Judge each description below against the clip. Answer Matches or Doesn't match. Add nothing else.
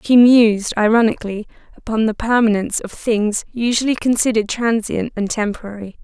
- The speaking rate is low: Matches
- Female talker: Matches